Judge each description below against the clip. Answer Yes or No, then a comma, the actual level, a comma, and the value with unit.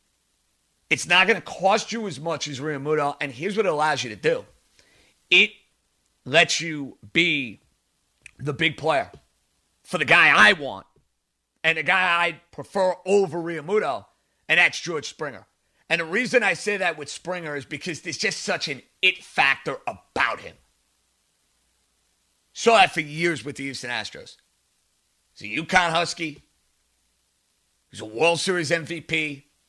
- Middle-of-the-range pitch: Yes, medium, 160 Hz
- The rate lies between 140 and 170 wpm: Yes, average, 155 wpm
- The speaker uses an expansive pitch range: Yes, wide, 6.0 semitones